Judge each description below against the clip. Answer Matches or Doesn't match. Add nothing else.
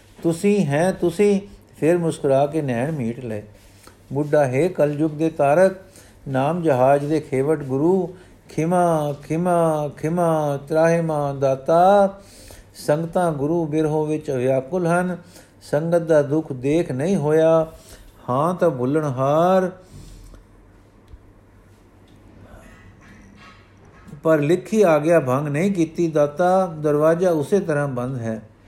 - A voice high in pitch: Doesn't match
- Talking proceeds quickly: Doesn't match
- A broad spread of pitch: Matches